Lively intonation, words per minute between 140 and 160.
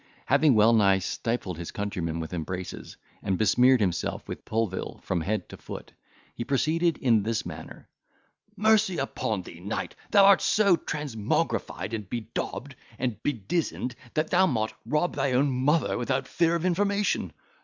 Yes: wide, 7.6 semitones; average, 155 wpm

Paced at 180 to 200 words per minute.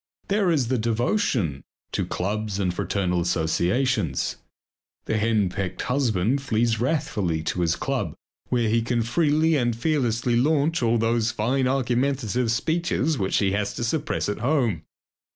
No: average, 140 wpm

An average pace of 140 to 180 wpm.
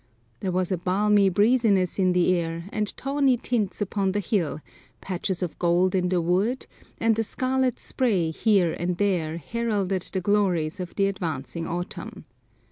Yes: average, 160 wpm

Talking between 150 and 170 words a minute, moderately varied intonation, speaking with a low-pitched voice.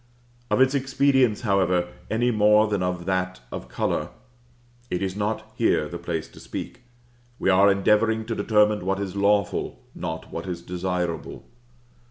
Yes: average, 155 wpm; average, 3.2 semitones; low, 100 Hz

